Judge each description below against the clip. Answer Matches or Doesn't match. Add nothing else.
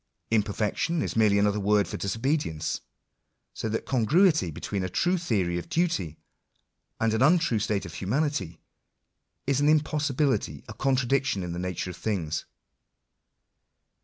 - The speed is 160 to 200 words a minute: Doesn't match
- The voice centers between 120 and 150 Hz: Doesn't match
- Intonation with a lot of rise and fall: Matches